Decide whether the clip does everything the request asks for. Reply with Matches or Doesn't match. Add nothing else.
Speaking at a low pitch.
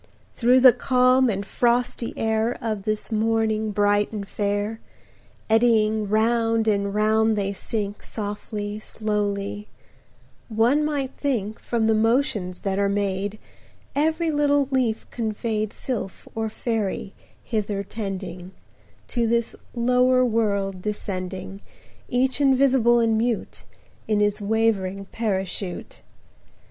Doesn't match